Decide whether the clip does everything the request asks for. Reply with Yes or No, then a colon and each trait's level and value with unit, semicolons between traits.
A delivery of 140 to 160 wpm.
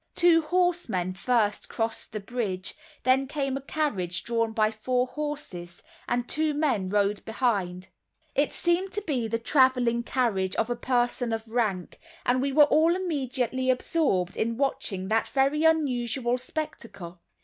Yes: average, 150 wpm